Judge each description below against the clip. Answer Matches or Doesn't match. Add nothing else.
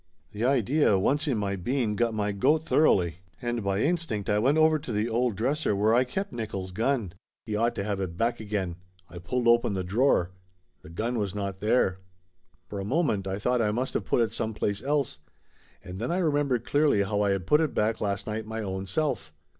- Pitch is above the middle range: Doesn't match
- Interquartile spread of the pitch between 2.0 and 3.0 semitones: Doesn't match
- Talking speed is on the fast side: Matches